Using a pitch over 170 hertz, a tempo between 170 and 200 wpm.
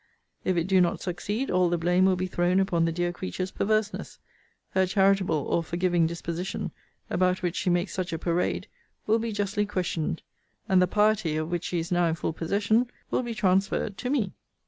Yes: medium, 185 Hz; average, 195 wpm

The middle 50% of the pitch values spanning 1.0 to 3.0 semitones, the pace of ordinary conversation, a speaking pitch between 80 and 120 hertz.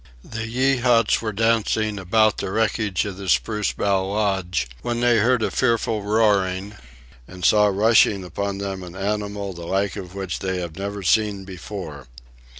Yes: narrow, 2.5 semitones; average, 160 wpm; low, 100 Hz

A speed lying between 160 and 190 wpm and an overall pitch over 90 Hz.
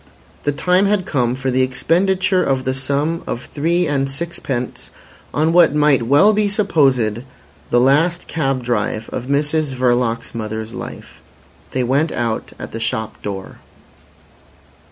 No: average, 145 wpm; low, 135 Hz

